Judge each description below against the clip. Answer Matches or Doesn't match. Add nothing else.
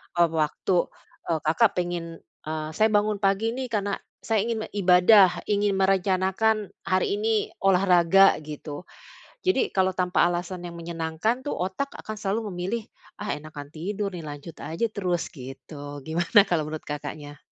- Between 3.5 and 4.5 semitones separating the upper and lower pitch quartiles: Matches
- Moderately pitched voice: Matches